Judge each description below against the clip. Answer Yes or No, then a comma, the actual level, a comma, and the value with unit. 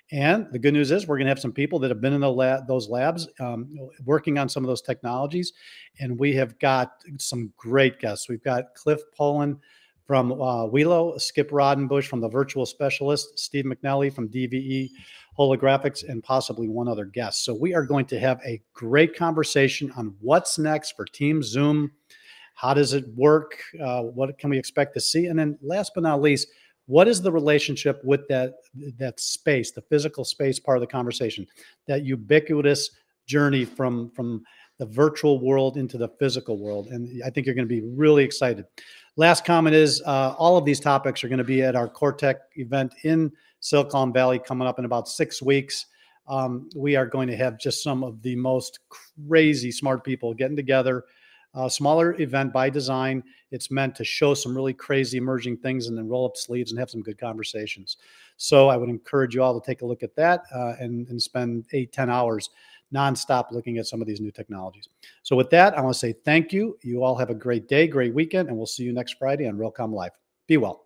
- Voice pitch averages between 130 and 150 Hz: Yes, low, 135 Hz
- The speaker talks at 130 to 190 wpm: No, fast, 205 wpm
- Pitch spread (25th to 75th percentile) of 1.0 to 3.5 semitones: Yes, average, 2.8 semitones